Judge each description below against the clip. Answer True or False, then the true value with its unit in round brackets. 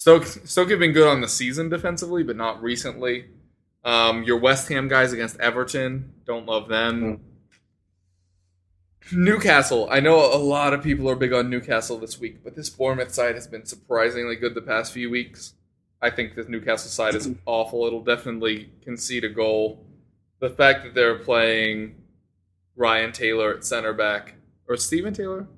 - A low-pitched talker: True (120 Hz)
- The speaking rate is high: False (170 wpm)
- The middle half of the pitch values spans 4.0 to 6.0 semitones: False (3.0 semitones)